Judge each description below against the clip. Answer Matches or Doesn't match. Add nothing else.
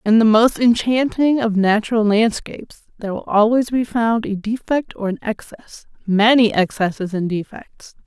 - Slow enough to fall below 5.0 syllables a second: Matches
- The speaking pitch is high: Matches